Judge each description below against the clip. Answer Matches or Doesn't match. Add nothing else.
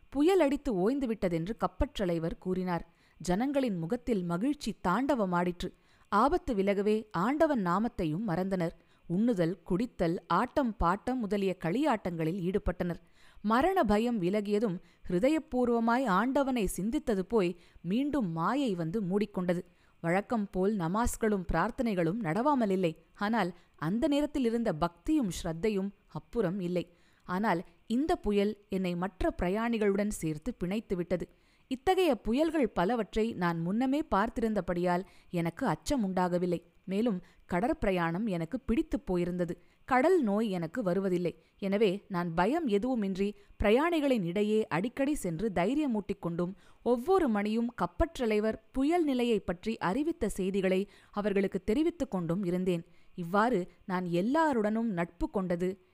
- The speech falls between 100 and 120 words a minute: Matches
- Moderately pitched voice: Doesn't match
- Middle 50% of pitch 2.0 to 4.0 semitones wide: Doesn't match